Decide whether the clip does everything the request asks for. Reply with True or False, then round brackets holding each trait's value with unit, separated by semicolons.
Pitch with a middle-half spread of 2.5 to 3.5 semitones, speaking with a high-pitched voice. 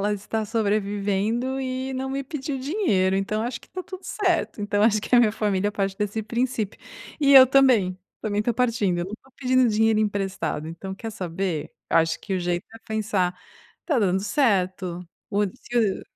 False (4.6 semitones; 215 Hz)